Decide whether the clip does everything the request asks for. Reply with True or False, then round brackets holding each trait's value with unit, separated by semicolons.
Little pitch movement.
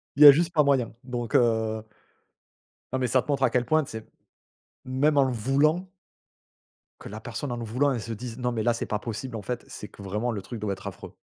False (3.5 semitones)